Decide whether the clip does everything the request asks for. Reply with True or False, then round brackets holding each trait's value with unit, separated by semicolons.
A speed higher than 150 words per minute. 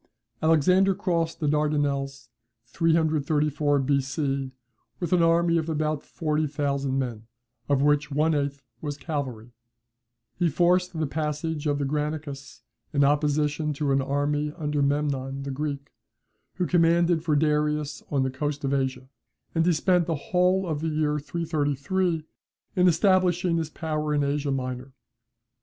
False (145 wpm)